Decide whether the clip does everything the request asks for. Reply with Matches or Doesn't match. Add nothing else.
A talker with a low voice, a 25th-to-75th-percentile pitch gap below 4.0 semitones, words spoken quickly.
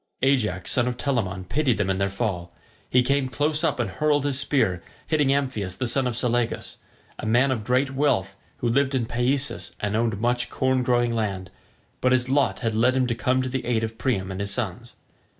Matches